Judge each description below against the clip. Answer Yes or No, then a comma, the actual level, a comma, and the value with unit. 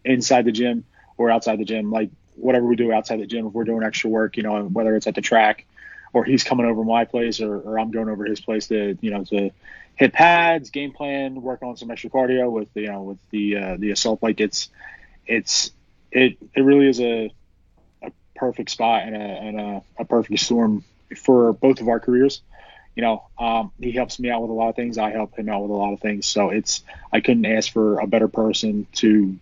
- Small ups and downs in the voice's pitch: Yes, narrow, 2.1 semitones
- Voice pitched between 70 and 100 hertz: No, low, 110 Hz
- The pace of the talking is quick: Yes, fast, 235 wpm